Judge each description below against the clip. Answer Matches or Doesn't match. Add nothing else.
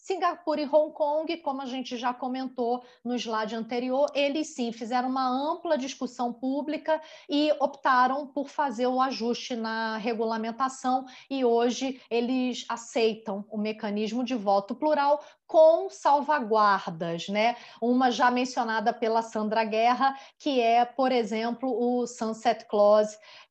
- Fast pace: Doesn't match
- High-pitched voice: Matches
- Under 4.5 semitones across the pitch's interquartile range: Matches